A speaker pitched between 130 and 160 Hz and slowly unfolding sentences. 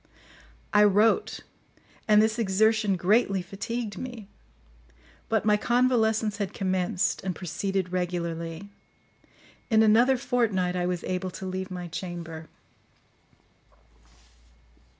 No: high, 195 Hz; slow, 105 wpm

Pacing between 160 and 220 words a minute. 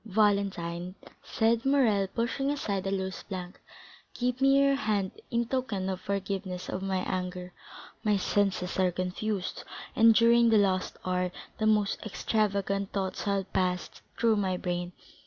No: average, 145 wpm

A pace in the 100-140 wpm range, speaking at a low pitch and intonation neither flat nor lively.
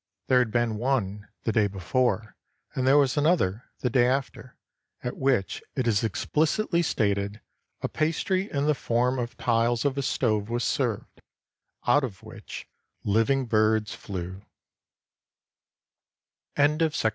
Yes: slow, 135 wpm; low, 120 Hz; average, 4.1 semitones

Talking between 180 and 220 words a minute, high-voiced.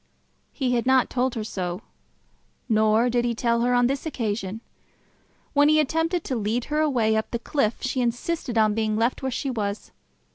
Yes: average, 185 wpm; high, 240 Hz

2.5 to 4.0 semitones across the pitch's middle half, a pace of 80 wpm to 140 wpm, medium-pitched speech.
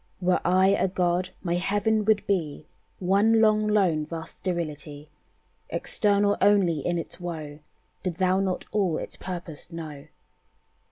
Yes: average, 3.4 semitones; slow, 135 wpm; medium, 180 Hz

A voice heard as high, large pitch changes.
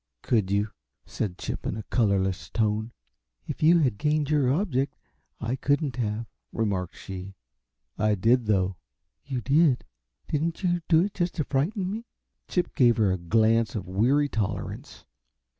No: low, 120 Hz; wide, 6.3 semitones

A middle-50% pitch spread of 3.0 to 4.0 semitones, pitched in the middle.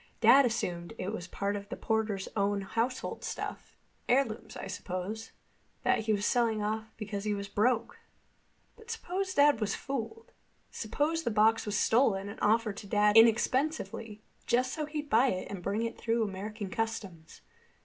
No: average, 3.3 semitones; high, 220 Hz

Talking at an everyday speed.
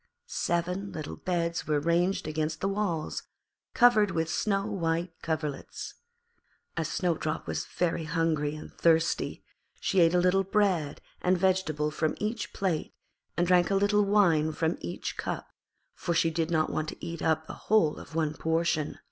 Yes: average, 160 wpm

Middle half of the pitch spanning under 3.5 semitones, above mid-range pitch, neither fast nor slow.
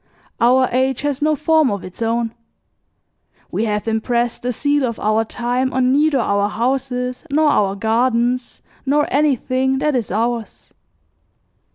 Yes: average, 2.9 semitones; very high, 250 Hz; average, 145 wpm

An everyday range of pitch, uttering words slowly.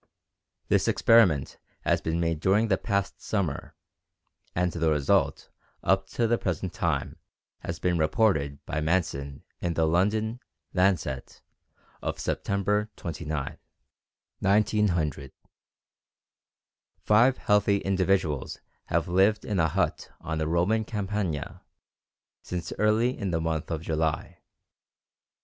Yes: average, 4.5 semitones; slow, 115 wpm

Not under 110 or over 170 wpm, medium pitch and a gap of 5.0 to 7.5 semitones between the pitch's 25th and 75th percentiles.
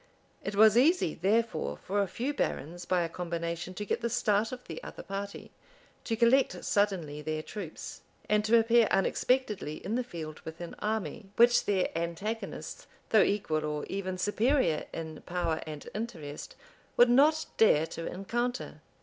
No: average, 160 wpm; high, 200 Hz; wide, 5.5 semitones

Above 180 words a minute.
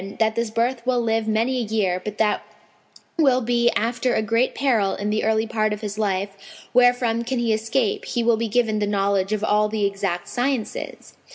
Yes: average, 200 wpm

